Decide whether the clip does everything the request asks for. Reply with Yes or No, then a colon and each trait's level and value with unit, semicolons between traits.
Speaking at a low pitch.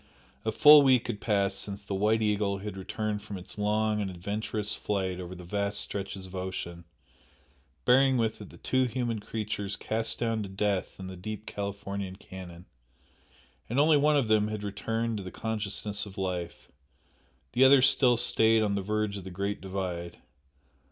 Yes: low, 105 Hz